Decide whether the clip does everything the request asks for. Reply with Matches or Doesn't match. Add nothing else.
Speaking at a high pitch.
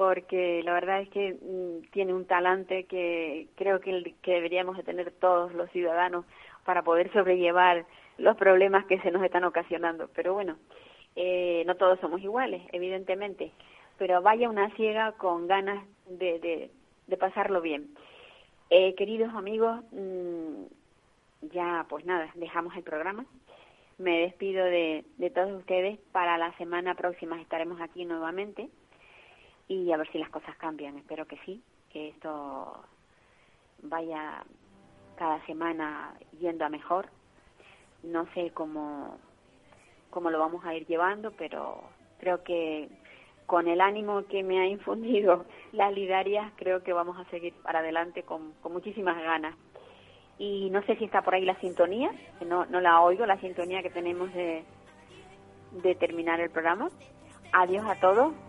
Doesn't match